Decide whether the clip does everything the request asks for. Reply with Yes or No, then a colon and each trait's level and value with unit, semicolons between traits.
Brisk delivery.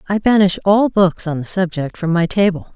Yes: fast, 215 wpm